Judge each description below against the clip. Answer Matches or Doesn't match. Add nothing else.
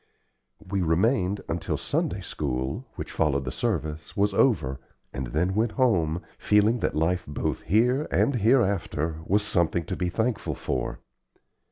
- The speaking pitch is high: Doesn't match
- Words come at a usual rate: Matches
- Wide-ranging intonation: Matches